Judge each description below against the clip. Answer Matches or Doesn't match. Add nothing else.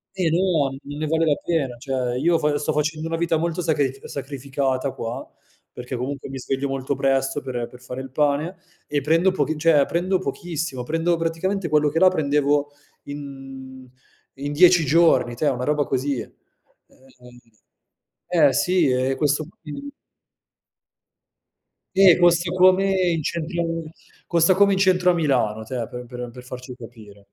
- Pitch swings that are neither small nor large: Matches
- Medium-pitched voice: Matches